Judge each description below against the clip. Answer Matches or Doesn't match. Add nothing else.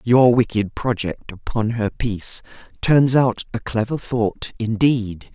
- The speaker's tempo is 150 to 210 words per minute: Doesn't match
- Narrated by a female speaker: Matches